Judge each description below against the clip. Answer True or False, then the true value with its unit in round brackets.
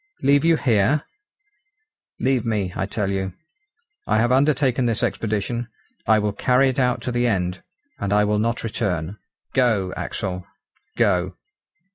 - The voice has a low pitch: True (110 Hz)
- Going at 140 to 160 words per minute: True (145 wpm)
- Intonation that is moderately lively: True (4.2 semitones)